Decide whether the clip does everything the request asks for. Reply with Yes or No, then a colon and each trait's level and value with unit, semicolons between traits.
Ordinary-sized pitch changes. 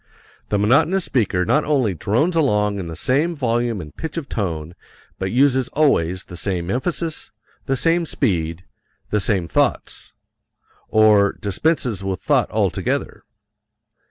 No: wide, 7.3 semitones